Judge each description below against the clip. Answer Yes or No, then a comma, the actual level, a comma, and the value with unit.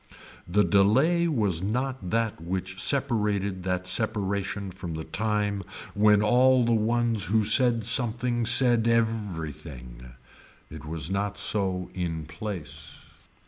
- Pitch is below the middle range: Yes, low, 105 Hz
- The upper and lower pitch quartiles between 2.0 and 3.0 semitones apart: No, average, 4.1 semitones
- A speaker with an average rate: No, slow, 125 wpm